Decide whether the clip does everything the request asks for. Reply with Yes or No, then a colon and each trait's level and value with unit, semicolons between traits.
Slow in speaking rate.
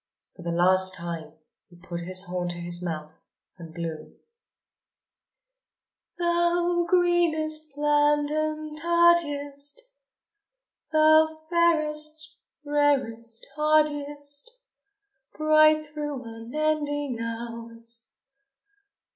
Yes: slow, 80 wpm